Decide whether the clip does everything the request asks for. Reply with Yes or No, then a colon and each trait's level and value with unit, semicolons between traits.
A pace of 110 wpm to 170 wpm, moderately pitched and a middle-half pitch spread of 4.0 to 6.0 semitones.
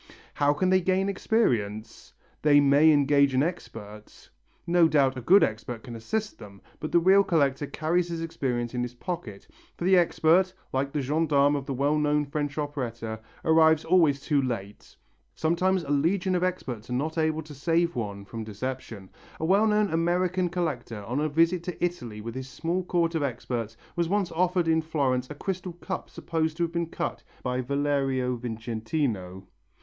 No: average, 180 wpm; medium, 150 Hz; wide, 5.4 semitones